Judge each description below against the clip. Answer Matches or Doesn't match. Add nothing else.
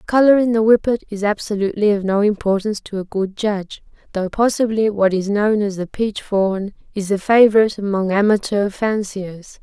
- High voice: Matches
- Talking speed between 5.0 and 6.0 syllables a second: Matches